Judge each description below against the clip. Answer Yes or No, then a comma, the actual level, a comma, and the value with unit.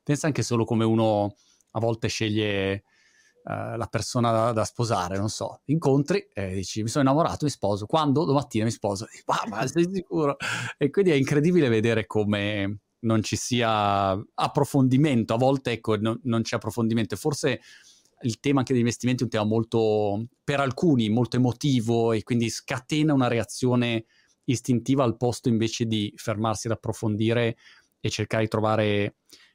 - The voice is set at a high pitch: No, low, 115 Hz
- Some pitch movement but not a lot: Yes, average, 3.6 semitones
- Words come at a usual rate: Yes, average, 160 wpm